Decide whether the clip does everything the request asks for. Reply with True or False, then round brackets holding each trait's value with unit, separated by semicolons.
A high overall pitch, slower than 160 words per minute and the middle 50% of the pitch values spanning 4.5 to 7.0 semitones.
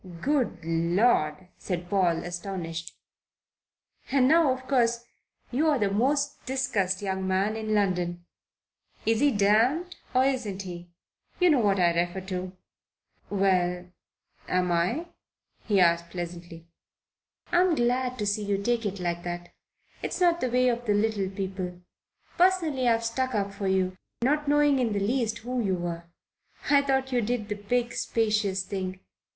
True (205 Hz; 150 wpm; 5.6 semitones)